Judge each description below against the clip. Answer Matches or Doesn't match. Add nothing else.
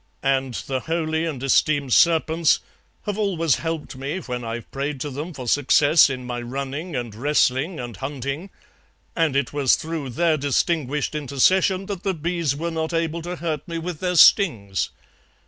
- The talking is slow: Doesn't match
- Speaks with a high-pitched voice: Doesn't match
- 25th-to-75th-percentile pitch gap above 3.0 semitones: Matches